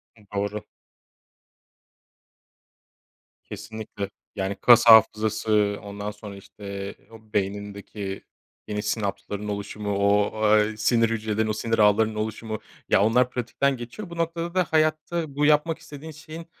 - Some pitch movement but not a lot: Yes, average, 3.5 semitones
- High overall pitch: No, low, 110 Hz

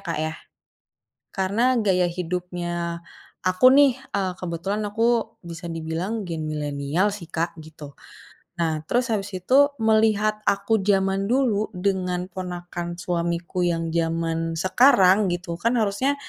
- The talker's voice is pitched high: No, medium, 180 Hz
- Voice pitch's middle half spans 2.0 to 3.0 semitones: No, average, 3.4 semitones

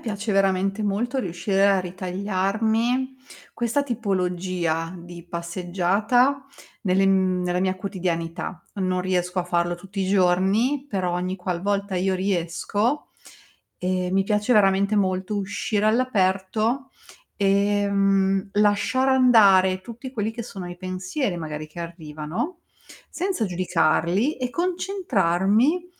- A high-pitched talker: Yes, high, 195 Hz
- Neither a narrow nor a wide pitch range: Yes, average, 3.2 semitones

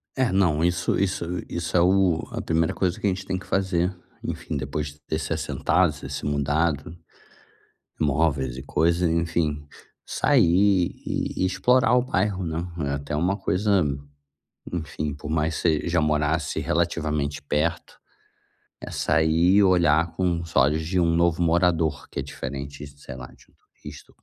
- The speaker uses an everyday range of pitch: Yes, average, 3.2 semitones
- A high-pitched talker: No, very low, 85 Hz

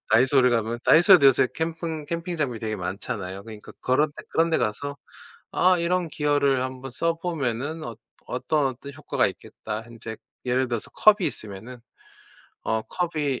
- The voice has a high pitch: No, low, 135 Hz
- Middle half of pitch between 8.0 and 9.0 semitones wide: No, wide, 5.9 semitones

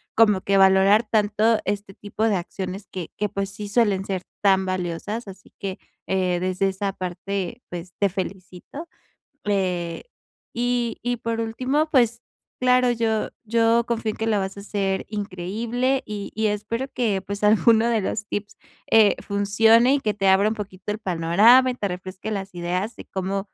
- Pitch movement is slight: No, average, 3.0 semitones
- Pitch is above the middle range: Yes, high, 205 Hz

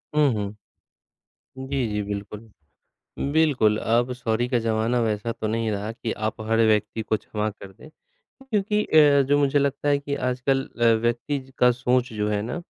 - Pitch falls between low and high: No, low, 120 Hz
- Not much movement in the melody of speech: No, average, 4.4 semitones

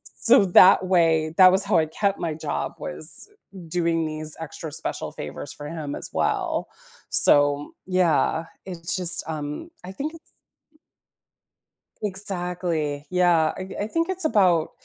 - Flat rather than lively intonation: No, average, 3.3 semitones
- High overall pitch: No, medium, 175 Hz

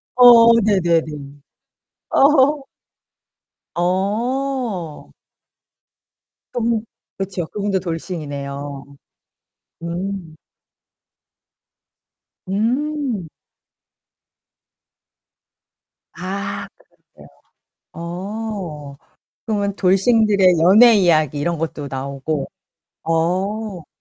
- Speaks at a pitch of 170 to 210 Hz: Yes, high, 190 Hz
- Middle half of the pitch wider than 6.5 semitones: No, average, 5.2 semitones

